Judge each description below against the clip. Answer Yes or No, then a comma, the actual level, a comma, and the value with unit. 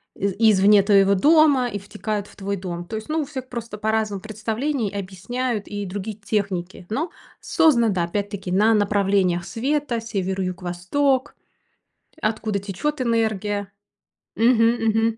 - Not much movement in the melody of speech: No, average, 3.0 semitones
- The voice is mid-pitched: No, high, 210 Hz